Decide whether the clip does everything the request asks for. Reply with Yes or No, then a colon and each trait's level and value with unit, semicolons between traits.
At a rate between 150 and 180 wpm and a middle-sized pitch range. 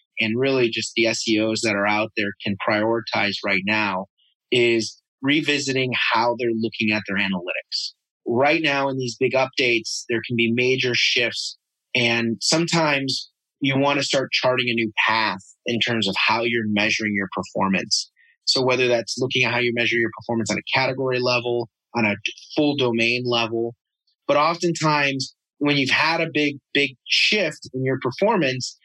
Yes: average, 170 wpm; average, 3.0 semitones